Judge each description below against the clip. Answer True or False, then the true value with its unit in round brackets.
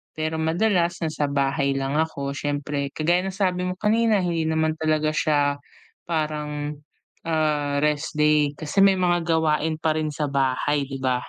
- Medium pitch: True (155 Hz)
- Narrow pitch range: True (2.2 semitones)